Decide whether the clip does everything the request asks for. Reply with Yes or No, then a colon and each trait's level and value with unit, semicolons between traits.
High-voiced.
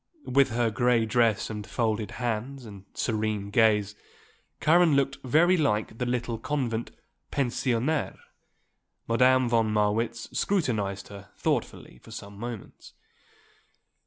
No: low, 115 Hz